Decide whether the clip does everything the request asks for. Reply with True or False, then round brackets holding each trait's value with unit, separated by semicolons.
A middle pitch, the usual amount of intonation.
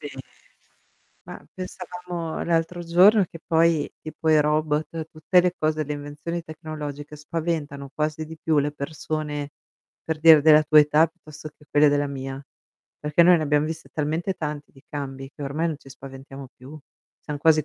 False (155 Hz; 1.9 semitones)